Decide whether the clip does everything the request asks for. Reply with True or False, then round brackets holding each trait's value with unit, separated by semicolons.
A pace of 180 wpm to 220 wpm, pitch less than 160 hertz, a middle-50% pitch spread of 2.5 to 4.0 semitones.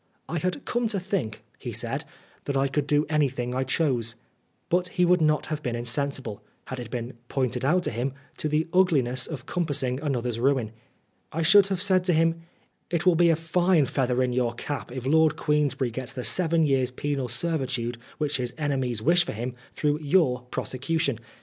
False (195 wpm; 140 Hz; 4.7 semitones)